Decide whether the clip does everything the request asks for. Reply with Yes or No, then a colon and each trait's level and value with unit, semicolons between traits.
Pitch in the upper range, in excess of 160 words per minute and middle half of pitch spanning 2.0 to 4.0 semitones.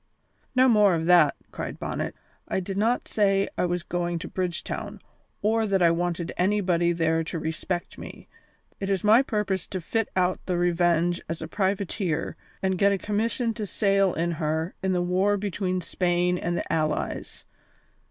No: medium, 180 Hz; average, 170 wpm; average, 2.7 semitones